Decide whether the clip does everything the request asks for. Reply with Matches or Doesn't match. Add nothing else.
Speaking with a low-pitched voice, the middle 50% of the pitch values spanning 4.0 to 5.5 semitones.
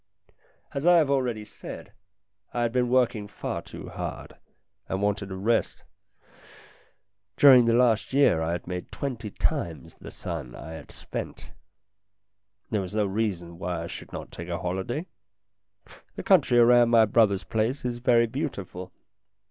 Matches